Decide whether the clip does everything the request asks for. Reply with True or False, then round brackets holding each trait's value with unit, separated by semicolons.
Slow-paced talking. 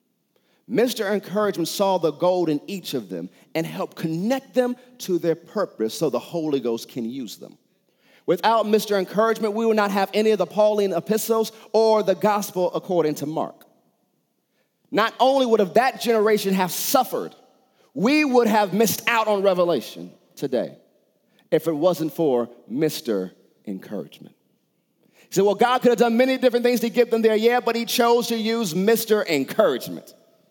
False (165 wpm)